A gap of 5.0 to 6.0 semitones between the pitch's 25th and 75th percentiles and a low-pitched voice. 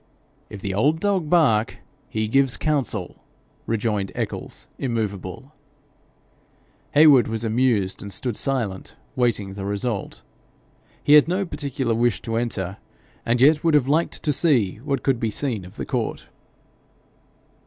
Yes: wide, 5.4 semitones; low, 120 Hz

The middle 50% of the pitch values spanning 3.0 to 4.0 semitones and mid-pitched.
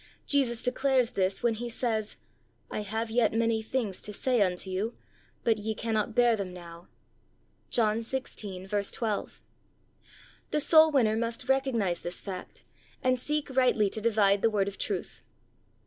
No: average, 3.3 semitones; high, 225 Hz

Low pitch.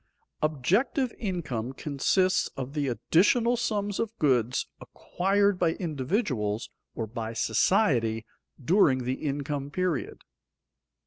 No: medium, 150 Hz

